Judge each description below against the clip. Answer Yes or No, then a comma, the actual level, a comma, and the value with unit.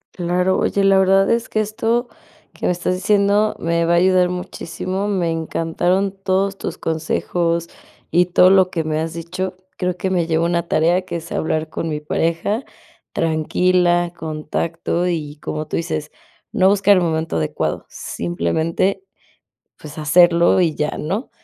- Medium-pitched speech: Yes, medium, 175 Hz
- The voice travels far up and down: No, narrow, 2.6 semitones